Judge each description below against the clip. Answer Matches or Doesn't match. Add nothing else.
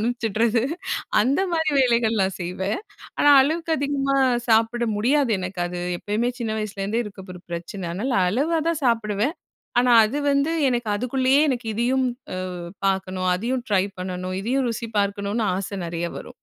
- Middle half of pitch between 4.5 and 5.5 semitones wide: Matches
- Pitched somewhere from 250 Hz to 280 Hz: Doesn't match